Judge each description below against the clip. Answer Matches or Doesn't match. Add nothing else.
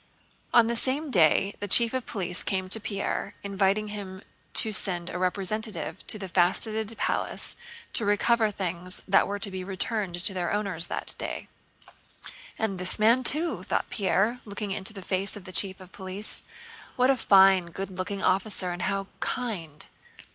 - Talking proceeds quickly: Doesn't match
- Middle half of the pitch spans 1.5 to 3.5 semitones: Matches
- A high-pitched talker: Matches